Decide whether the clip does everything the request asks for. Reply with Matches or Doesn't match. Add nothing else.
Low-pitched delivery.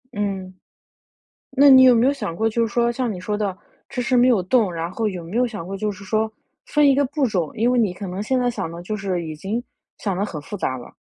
Doesn't match